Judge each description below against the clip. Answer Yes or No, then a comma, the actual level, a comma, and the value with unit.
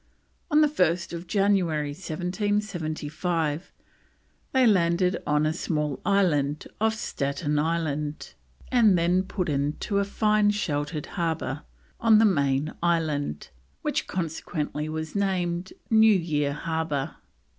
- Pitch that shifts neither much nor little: Yes, average, 4.7 semitones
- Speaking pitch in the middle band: Yes, medium, 170 Hz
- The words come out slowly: Yes, slow, 115 wpm